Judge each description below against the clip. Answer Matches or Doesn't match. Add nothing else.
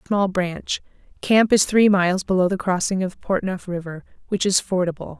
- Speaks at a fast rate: Doesn't match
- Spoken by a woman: Matches